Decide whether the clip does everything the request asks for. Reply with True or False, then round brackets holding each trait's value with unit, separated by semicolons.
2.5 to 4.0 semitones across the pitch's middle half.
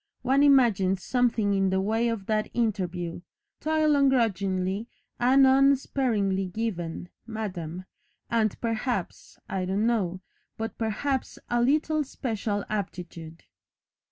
False (4.7 semitones)